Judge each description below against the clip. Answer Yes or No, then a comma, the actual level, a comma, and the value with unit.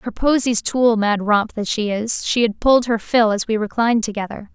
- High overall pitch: Yes, high, 225 Hz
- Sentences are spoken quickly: Yes, fast, 225 wpm